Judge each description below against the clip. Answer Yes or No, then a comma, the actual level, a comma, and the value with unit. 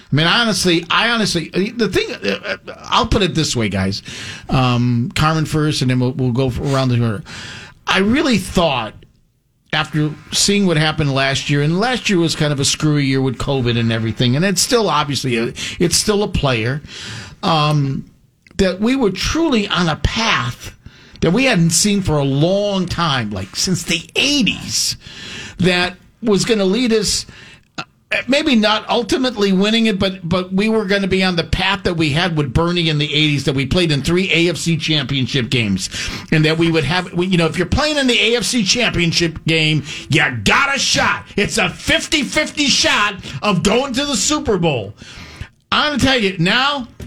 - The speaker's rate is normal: Yes, average, 190 wpm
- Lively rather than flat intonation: Yes, wide, 6.7 semitones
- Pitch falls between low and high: Yes, medium, 170 Hz